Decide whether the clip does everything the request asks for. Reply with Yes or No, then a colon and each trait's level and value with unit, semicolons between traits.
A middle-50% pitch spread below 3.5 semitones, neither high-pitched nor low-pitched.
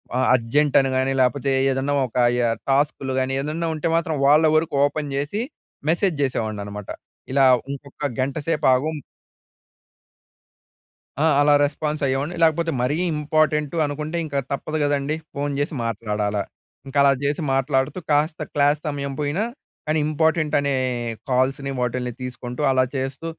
Yes: narrow, 2.6 semitones; medium, 145 Hz